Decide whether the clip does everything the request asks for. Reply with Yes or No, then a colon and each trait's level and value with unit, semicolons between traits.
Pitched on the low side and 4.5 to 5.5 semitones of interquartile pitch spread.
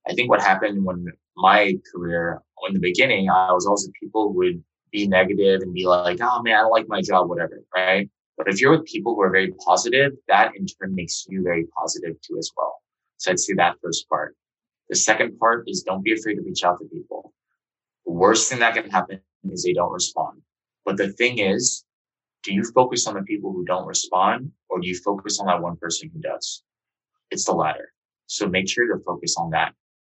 No: very low, 95 Hz; average, 3.9 semitones